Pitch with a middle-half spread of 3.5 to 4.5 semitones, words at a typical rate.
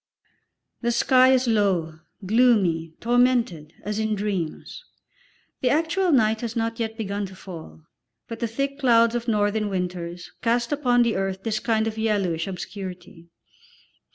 Yes: average, 4.2 semitones; average, 145 wpm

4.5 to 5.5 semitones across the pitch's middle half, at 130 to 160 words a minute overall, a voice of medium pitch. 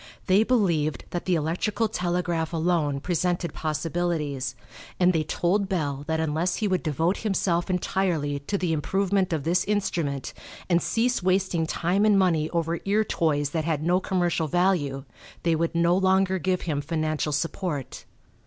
No: average, 3.2 semitones; average, 155 wpm; medium, 170 Hz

